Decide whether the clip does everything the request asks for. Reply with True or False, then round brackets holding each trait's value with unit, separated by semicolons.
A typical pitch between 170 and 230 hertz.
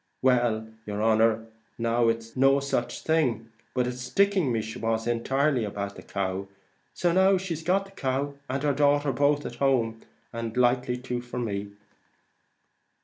False (125 Hz)